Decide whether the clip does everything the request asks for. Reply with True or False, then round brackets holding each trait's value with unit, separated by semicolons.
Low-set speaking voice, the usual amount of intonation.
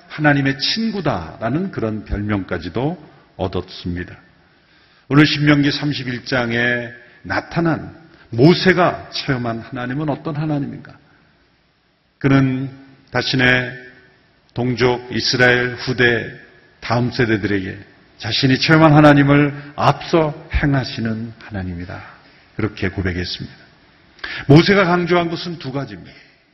True (130 Hz; 4.7 semitones)